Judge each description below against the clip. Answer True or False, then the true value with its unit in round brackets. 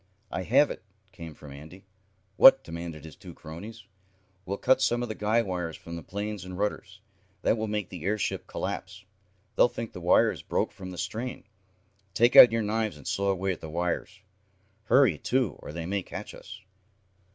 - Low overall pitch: True (95 Hz)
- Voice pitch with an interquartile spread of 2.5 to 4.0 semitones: False (4.4 semitones)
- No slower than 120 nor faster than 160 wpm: False (185 wpm)